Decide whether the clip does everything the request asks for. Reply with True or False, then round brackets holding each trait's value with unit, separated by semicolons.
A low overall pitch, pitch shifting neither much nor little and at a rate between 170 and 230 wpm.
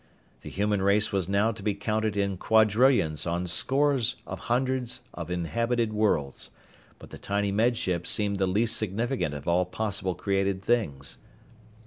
False (100 Hz; 3.7 semitones; 155 wpm)